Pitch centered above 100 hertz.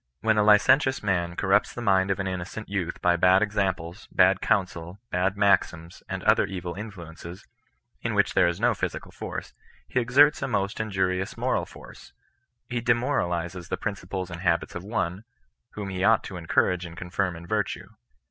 No: very low, 95 Hz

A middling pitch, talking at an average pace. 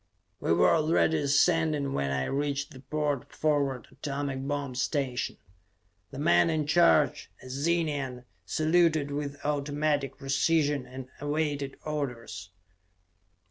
No: medium, 145 Hz; slow, 115 wpm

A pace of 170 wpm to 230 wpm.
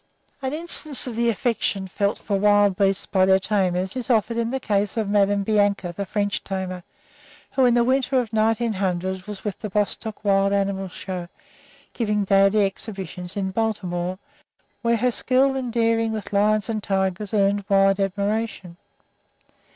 No: average, 160 wpm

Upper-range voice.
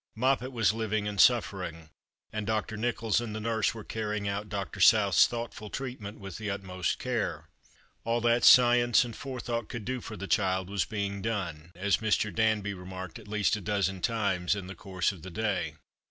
No: low, 105 Hz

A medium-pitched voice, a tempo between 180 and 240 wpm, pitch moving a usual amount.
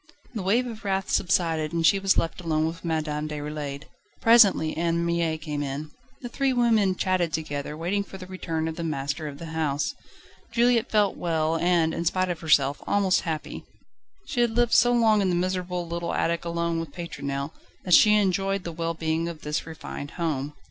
Yes: medium, 170 Hz; average, 190 wpm; average, 3.4 semitones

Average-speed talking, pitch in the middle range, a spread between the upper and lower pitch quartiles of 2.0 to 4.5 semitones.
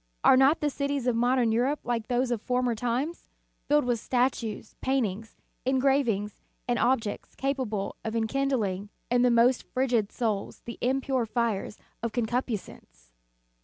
No: average, 145 wpm; high, 245 Hz; average, 2.9 semitones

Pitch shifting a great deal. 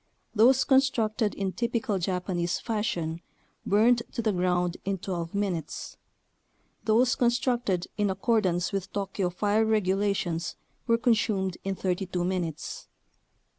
No: average, 3.9 semitones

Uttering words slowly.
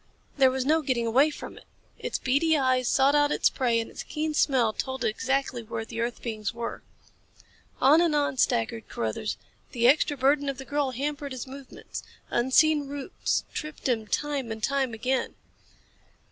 No: average, 175 wpm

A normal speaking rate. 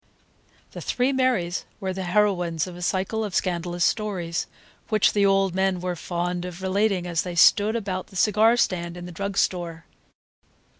Yes: average, 170 wpm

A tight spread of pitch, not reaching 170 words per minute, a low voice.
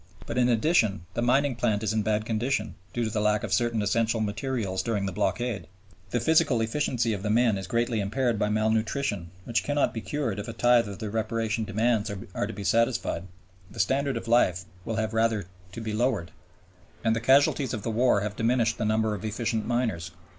No: narrow, 2.3 semitones; fast, 205 wpm; low, 115 Hz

